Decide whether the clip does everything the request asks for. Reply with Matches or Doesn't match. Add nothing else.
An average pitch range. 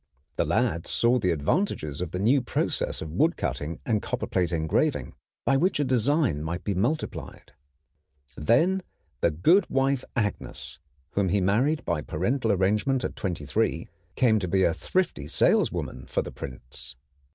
Doesn't match